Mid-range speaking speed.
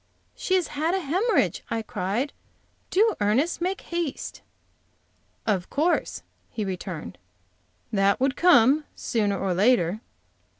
No: slow, 120 wpm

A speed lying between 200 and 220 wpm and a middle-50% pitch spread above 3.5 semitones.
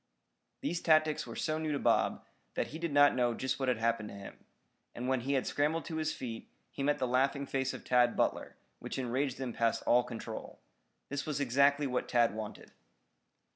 No: fast, 205 wpm; average, 3.1 semitones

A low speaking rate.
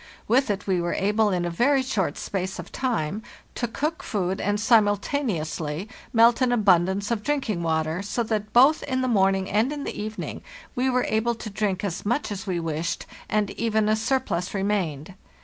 No: average, 190 wpm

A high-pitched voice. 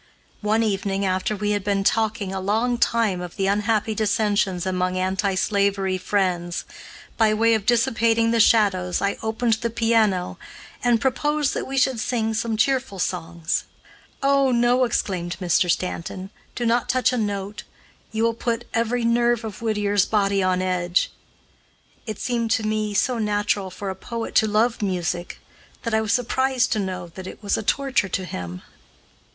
Yes: high, 210 Hz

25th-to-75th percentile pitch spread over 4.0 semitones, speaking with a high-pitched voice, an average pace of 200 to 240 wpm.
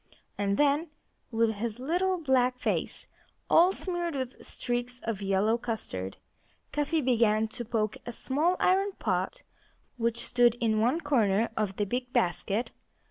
No: average, 5.0 semitones; high, 240 Hz; average, 140 wpm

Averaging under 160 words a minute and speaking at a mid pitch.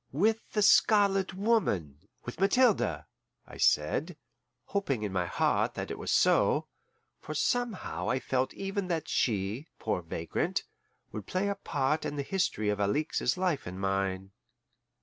Yes: average, 150 wpm; medium, 145 Hz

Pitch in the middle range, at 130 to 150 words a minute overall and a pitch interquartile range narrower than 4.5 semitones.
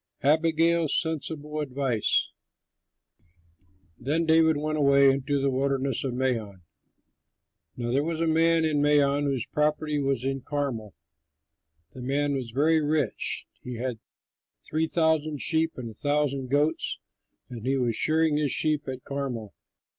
Yes: medium, 145 Hz; average, 140 wpm; average, 3.0 semitones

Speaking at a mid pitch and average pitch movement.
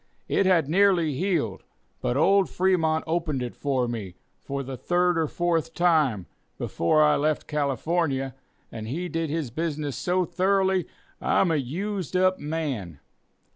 Yes: medium, 160 Hz; average, 4.6 semitones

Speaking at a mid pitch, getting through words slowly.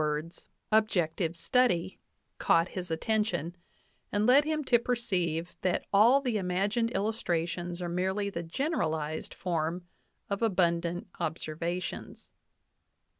Yes: medium, 180 Hz; slow, 115 wpm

